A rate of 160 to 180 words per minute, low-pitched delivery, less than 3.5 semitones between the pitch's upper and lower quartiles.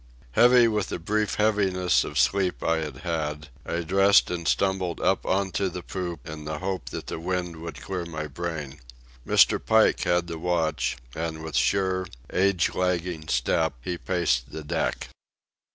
Yes: average, 170 wpm; very low, 85 Hz; average, 2.9 semitones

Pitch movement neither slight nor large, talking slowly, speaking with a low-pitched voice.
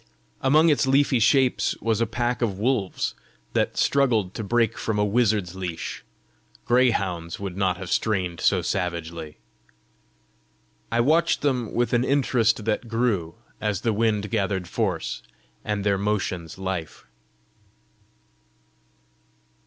Yes: average, 4.3 semitones; slow, 125 wpm; low, 105 Hz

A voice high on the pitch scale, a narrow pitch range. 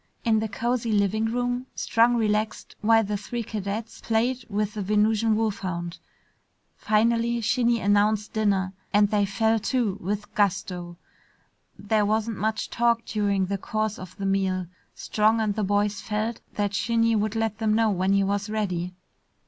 Yes: high, 215 Hz; narrow, 2.0 semitones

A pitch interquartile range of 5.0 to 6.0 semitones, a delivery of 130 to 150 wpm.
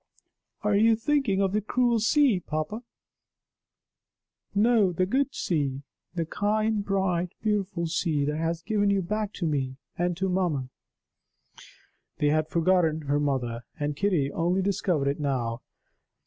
Yes: wide, 5.5 semitones; average, 145 wpm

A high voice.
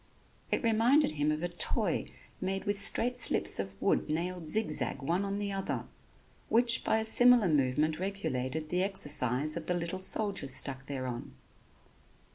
No: medium, 175 Hz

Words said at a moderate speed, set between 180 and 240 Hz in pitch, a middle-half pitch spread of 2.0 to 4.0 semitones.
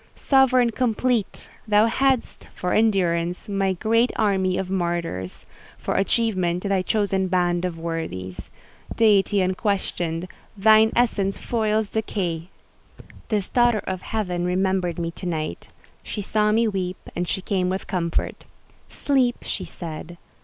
No: slow, 130 wpm; high, 190 Hz; average, 3.7 semitones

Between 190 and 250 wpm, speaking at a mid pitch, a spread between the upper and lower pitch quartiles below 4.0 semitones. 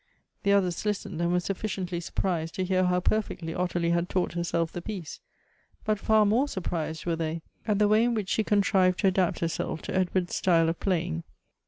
Yes: average, 200 wpm; medium, 180 Hz; average, 2.9 semitones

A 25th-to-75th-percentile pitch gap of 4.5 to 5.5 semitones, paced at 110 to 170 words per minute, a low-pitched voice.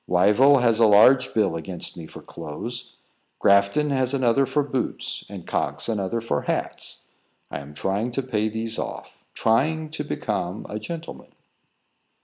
Yes: average, 5.1 semitones; average, 145 wpm; low, 115 Hz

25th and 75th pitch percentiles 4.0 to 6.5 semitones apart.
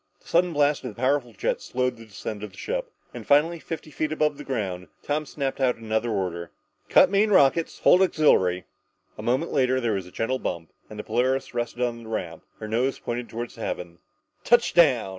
Yes: average, 5.3 semitones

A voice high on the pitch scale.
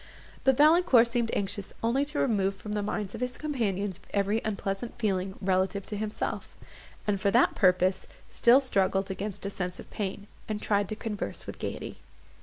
Yes: high, 205 Hz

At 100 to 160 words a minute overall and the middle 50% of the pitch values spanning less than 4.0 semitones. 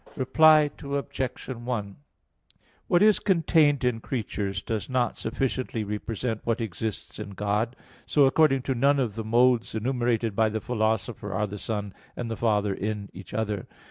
Yes: average, 155 wpm; average, 3.6 semitones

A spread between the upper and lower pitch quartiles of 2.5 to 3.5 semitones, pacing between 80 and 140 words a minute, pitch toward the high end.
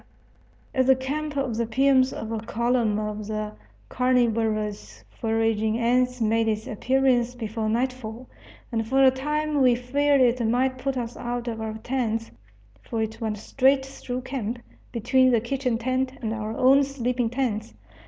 No: average, 2.8 semitones; average, 155 wpm; high, 240 Hz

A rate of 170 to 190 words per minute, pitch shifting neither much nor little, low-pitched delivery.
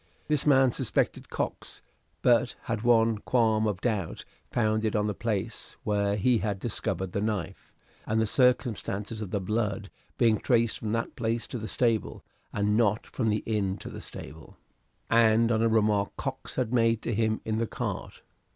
No: average, 175 wpm; narrow, 1.9 semitones; low, 110 Hz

